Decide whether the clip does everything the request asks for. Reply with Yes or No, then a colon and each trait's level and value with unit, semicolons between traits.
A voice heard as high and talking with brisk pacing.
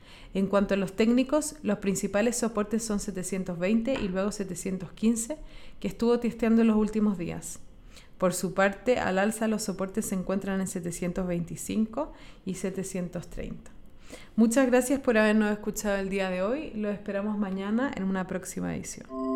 No: high, 200 Hz; average, 150 wpm